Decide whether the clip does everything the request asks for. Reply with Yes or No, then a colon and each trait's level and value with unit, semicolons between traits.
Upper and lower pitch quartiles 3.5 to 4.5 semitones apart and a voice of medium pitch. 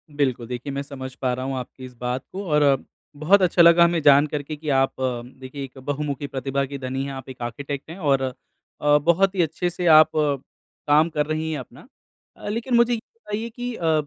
Yes: average, 3.9 semitones; medium, 145 Hz